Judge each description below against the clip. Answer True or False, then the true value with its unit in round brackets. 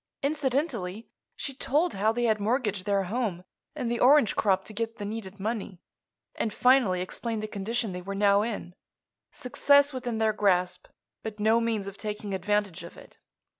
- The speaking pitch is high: True (215 Hz)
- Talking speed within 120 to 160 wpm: False (170 wpm)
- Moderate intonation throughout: True (3.3 semitones)